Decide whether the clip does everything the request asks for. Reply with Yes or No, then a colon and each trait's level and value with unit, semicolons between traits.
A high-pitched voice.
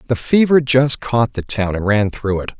No: low, 120 Hz